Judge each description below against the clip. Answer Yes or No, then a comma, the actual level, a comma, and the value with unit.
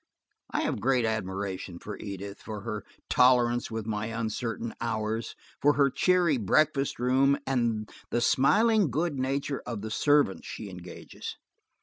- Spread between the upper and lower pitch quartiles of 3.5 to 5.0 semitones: Yes, average, 4.3 semitones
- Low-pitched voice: Yes, low, 115 Hz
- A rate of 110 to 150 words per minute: Yes, average, 140 wpm